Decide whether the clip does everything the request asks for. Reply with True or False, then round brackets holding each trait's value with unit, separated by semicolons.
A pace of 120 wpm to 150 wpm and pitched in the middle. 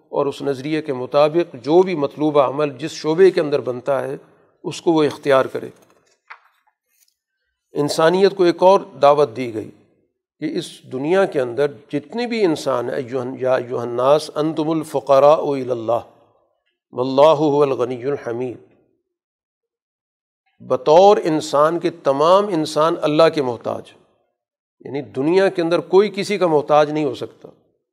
True (130 wpm; 150 Hz)